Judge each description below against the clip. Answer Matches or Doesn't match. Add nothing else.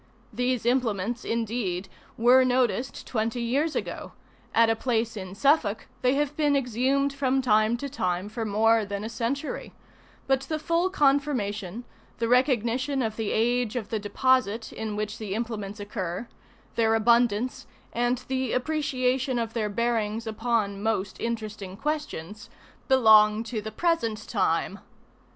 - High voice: Matches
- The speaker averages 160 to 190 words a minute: Doesn't match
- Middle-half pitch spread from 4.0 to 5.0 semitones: Doesn't match